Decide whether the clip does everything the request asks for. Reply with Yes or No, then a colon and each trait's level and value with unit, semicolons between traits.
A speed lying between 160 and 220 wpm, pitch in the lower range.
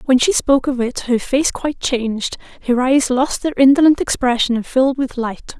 No: fast, 205 wpm; very high, 260 Hz